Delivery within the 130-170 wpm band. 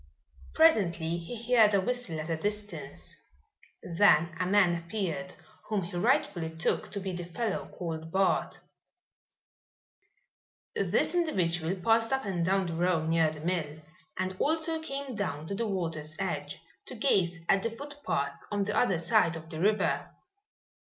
Yes: average, 150 wpm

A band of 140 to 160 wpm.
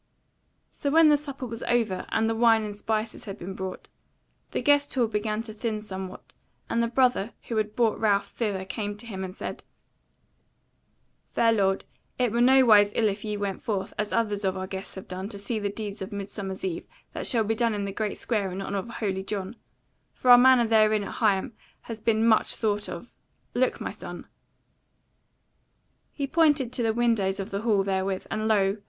No: average, 200 wpm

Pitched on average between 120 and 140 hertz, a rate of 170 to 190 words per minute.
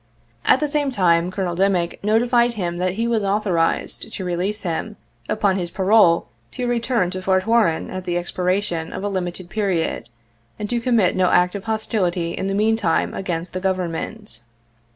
No: high, 190 Hz; average, 175 wpm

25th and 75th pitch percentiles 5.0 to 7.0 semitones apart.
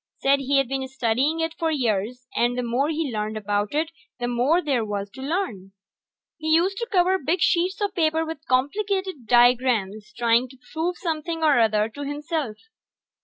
Yes: wide, 5.5 semitones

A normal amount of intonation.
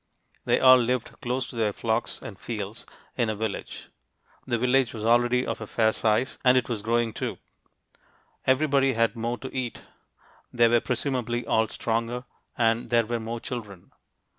No: narrow, 1.9 semitones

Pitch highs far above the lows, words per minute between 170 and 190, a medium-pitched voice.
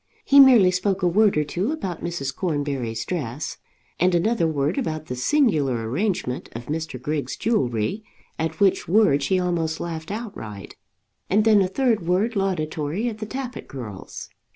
No: wide, 6.4 semitones; average, 160 wpm; medium, 175 Hz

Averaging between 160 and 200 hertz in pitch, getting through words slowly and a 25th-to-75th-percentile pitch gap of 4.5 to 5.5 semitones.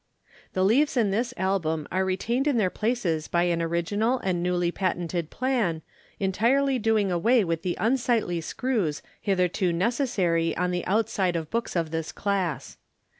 No: high, 190 Hz; average, 155 wpm; average, 4.9 semitones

